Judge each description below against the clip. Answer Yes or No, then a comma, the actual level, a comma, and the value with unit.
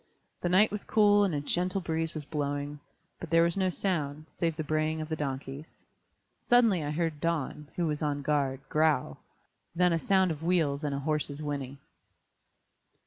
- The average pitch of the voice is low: No, medium, 155 Hz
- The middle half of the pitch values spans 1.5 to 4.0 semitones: Yes, average, 3.2 semitones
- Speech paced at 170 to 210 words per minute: Yes, average, 180 wpm